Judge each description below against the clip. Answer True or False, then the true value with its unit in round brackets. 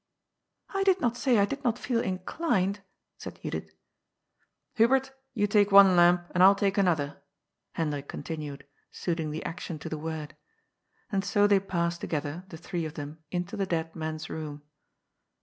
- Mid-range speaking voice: True (180 Hz)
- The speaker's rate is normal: True (165 wpm)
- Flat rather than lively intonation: False (4.4 semitones)